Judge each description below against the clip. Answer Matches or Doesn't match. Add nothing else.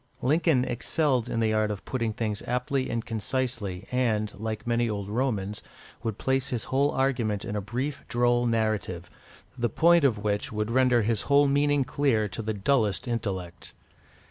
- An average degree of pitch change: Matches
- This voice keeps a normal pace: Matches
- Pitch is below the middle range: Matches